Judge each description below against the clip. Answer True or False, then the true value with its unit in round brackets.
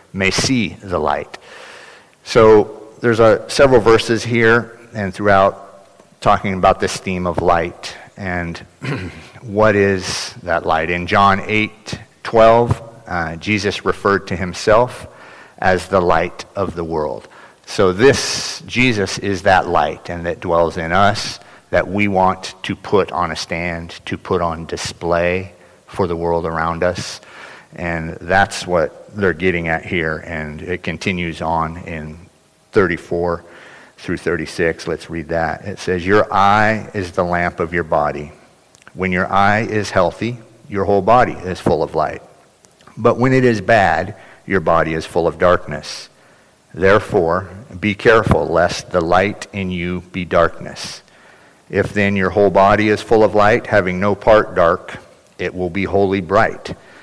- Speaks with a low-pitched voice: True (95 Hz)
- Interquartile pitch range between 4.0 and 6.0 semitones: False (3.2 semitones)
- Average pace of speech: True (155 wpm)